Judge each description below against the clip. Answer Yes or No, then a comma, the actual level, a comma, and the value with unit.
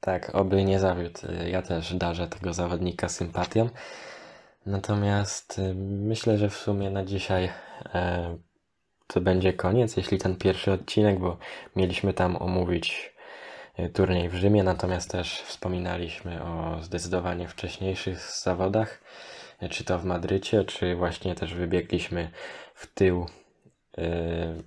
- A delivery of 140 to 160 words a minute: No, average, 115 wpm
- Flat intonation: Yes, narrow, 1.7 semitones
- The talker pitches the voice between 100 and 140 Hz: No, very low, 90 Hz